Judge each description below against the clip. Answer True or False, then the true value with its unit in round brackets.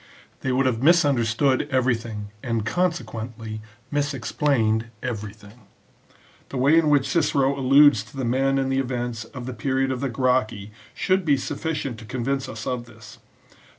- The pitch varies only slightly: False (3.2 semitones)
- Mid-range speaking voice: False (130 Hz)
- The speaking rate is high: False (155 wpm)